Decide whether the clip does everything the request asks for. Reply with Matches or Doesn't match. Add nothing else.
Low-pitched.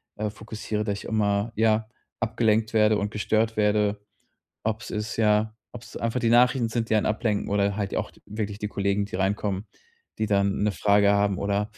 Matches